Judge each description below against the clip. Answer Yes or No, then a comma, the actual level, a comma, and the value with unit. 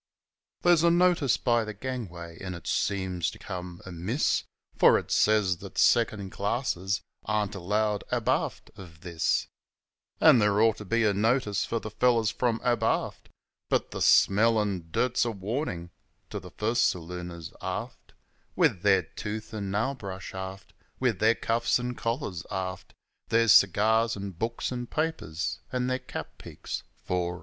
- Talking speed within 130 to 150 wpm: No, average, 160 wpm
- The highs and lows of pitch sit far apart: No, average, 3.9 semitones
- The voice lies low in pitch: Yes, low, 105 Hz